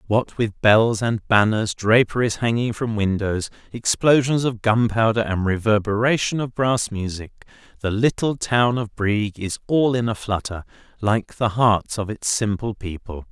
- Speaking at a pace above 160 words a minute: No, average, 155 wpm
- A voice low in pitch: Yes, low, 110 Hz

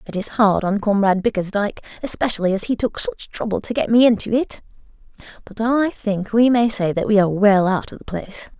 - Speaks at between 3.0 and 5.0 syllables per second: No, 5.8 syllables/s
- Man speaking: No, female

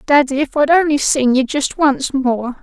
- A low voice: No, very high, 275 Hz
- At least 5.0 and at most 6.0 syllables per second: No, 4.4 syllables/s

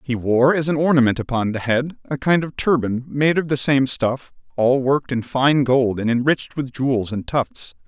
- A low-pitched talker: Yes, low, 130 Hz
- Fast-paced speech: Yes, fast, 215 wpm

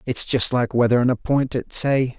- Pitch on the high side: No, low, 125 Hz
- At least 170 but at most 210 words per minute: No, fast, 220 wpm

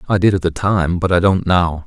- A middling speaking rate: No, fast, 290 wpm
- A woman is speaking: No, male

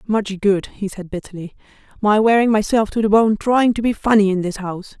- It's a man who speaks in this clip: No, female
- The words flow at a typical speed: No, fast, 215 wpm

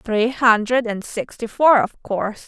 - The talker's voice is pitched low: No, high, 230 Hz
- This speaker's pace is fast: No, average, 170 wpm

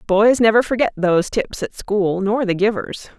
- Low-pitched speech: No, high, 210 Hz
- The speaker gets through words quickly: No, average, 190 wpm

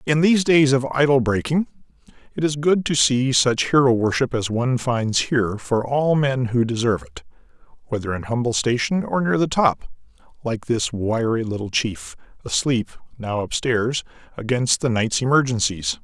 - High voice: No, low, 125 Hz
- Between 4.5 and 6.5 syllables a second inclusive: Yes, 4.9 syllables/s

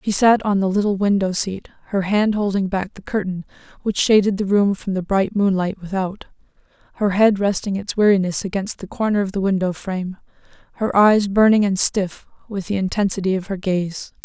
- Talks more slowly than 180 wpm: No, average, 190 wpm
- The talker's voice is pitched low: No, high, 195 Hz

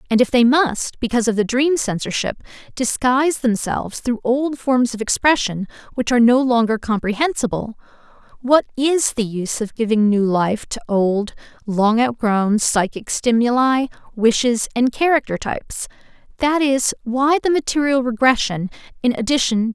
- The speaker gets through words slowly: No, average, 150 wpm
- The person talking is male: No, female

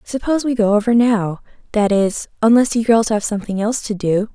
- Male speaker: No, female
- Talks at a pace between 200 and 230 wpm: Yes, fast, 205 wpm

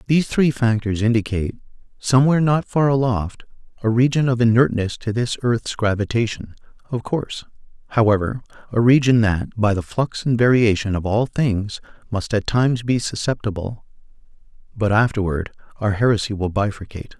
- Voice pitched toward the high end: No, low, 115 Hz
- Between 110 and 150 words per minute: Yes, average, 140 wpm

